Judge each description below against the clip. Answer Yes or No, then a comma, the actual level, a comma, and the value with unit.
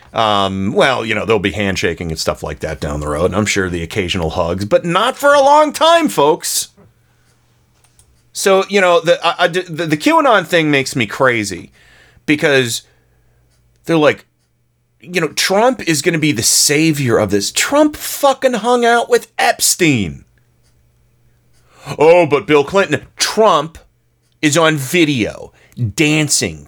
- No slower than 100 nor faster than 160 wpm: Yes, average, 155 wpm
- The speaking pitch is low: No, medium, 145 Hz